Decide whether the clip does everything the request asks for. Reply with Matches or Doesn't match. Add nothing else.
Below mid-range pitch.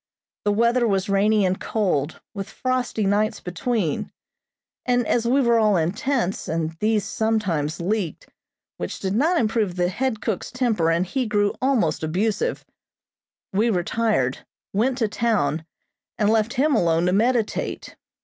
Doesn't match